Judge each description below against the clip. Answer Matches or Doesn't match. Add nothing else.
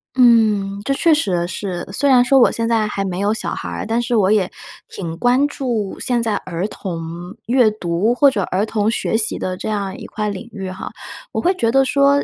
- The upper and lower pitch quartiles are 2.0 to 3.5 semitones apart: Doesn't match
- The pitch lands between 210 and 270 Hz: Matches